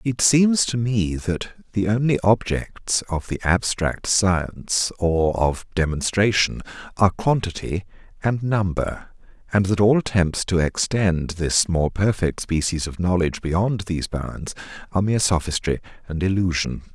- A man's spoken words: Yes, male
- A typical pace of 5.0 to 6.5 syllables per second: No, 4.3 syllables/s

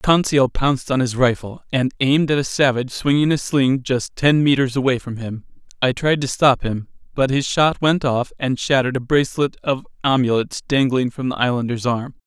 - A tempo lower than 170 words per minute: No, average, 195 wpm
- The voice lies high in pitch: No, low, 130 Hz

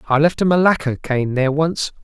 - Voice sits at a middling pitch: Yes, medium, 150 Hz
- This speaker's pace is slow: No, fast, 205 wpm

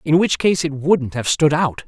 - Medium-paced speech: No, fast, 255 wpm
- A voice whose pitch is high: No, medium, 155 Hz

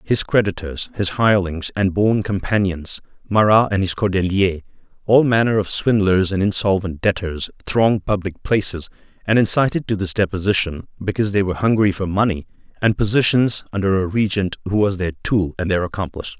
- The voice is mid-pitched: No, low, 100 Hz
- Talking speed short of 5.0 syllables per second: No, 5.5 syllables/s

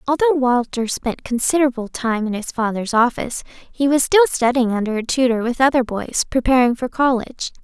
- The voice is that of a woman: Yes, female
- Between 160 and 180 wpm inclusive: Yes, average, 175 wpm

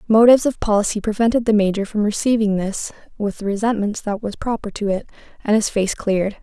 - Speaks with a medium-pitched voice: No, high, 210 Hz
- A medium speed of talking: Yes, average, 195 wpm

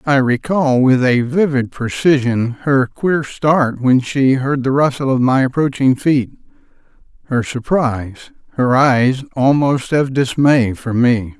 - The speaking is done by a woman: No, male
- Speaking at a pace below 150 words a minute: Yes, average, 140 wpm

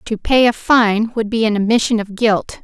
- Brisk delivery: Yes, fast, 230 wpm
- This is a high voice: Yes, high, 220 Hz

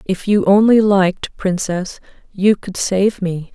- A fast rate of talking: No, average, 150 wpm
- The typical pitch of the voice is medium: No, high, 195 Hz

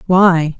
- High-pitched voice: No, medium, 175 Hz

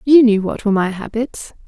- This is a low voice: No, high, 220 Hz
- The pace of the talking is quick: Yes, fast, 215 wpm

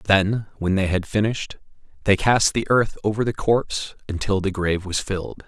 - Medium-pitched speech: No, low, 100 Hz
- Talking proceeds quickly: No, average, 185 wpm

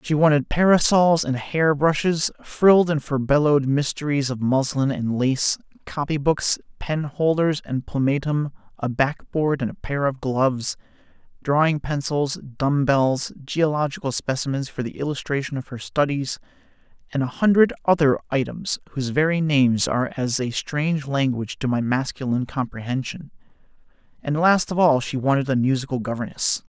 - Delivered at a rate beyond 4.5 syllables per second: Yes, 5.0 syllables/s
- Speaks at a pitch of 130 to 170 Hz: Yes, medium, 140 Hz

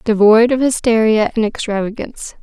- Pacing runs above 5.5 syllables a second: No, 5.3 syllables/s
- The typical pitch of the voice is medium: No, high, 225 Hz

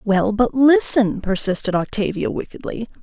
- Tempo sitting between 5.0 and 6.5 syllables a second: No, 4.6 syllables/s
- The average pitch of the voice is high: Yes, high, 220 Hz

